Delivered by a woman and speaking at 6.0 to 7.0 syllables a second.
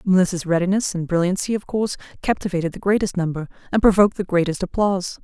Yes: female; 6.5 syllables/s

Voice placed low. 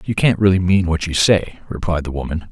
Yes: very low, 90 Hz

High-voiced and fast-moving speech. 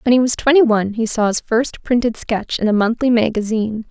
Yes: high, 230 Hz; fast, 230 wpm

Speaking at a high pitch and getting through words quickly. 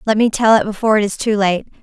Yes: high, 210 Hz; fast, 295 wpm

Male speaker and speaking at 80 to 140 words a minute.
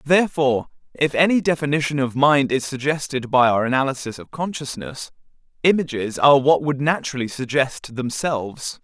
Yes: male; slow, 135 wpm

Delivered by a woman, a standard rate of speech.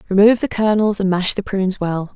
No: female; fast, 225 wpm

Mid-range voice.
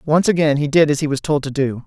Yes: medium, 145 Hz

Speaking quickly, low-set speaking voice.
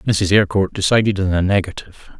No: average, 165 wpm; low, 100 Hz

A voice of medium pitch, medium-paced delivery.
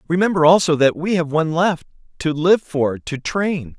Yes: medium, 160 Hz; average, 190 wpm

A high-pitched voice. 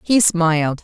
No: medium, 175 Hz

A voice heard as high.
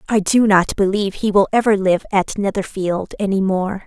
Yes: high, 200 Hz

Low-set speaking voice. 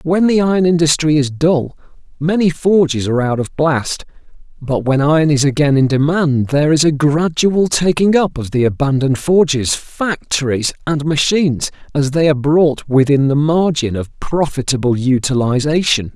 No: medium, 150 Hz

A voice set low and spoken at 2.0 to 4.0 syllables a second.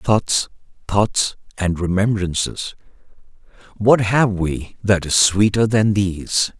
Yes: low, 100 Hz; 3.5 syllables/s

